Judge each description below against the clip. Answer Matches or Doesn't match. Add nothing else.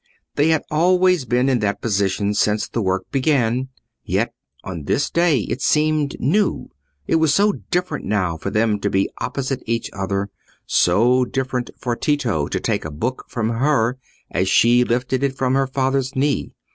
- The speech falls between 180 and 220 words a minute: Doesn't match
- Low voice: Matches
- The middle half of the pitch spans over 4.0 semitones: Matches